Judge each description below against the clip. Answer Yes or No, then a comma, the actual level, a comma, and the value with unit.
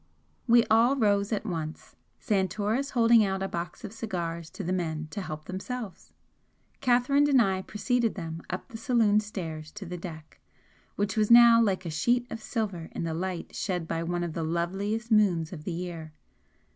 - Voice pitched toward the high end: Yes, high, 195 Hz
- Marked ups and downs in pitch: No, average, 4.9 semitones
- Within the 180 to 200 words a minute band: Yes, average, 185 wpm